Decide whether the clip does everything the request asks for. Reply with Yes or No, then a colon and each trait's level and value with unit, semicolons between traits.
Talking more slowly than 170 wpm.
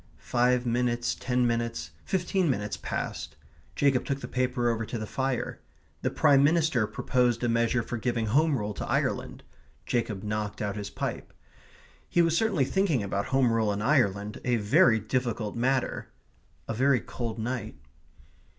Yes: average, 160 wpm